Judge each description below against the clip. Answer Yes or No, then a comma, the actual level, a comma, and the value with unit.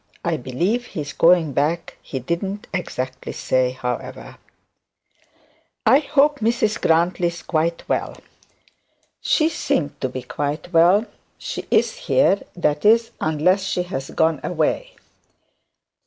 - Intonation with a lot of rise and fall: Yes, wide, 5.7 semitones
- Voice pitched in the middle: Yes, medium, 170 Hz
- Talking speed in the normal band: No, slow, 125 wpm